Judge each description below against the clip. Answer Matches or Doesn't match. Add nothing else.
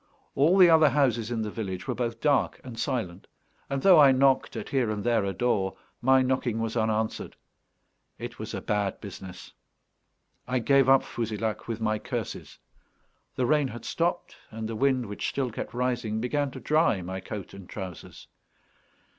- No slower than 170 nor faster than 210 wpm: Matches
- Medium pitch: Doesn't match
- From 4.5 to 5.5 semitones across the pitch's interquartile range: Doesn't match